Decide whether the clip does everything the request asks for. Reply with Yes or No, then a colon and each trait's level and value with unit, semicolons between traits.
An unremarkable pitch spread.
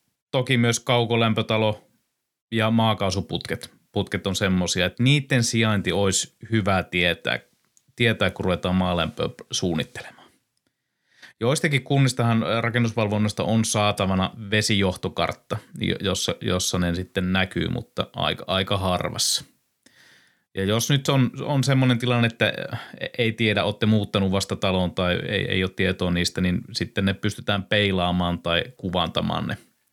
Yes: average, 3.8 semitones